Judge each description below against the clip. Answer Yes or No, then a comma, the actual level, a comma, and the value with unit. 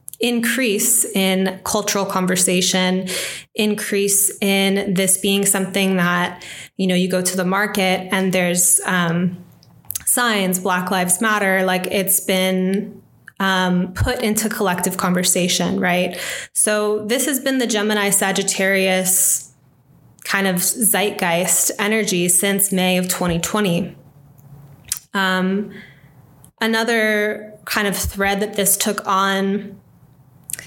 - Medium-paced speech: No, slow, 110 wpm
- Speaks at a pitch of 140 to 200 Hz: Yes, high, 190 Hz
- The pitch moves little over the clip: Yes, narrow, 2.1 semitones